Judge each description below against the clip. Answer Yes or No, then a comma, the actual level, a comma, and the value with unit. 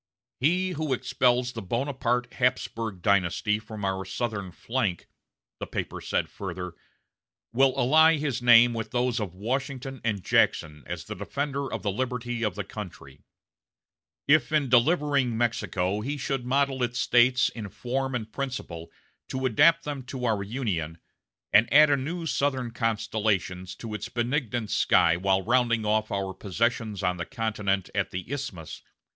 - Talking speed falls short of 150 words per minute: No, average, 155 wpm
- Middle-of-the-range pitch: No, low, 120 Hz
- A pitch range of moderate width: Yes, average, 4.6 semitones